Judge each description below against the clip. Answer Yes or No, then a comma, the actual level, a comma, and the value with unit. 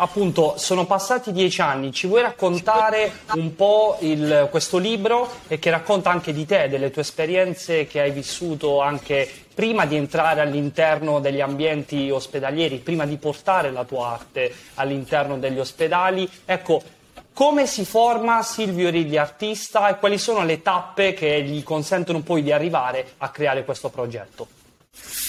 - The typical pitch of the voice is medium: Yes, medium, 160 Hz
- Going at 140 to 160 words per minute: Yes, average, 150 wpm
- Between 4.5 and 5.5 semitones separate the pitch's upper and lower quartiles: Yes, average, 5.2 semitones